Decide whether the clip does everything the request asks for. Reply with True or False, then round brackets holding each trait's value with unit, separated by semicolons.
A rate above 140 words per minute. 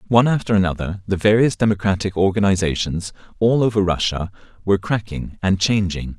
False (135 wpm)